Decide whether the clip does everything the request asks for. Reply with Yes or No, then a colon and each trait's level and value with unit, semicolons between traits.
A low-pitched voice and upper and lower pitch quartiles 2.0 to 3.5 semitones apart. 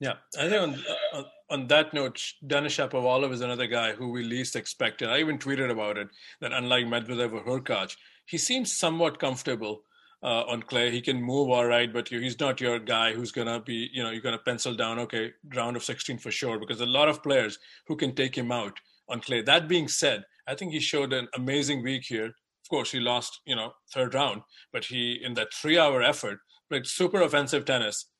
Yes: low, 125 Hz; average, 3.0 semitones